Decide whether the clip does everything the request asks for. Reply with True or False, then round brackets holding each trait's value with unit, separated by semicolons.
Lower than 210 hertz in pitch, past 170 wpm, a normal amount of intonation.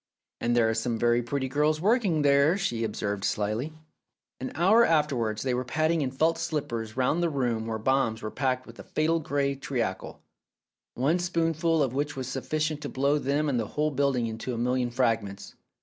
True (135 Hz; 190 wpm; 4.6 semitones)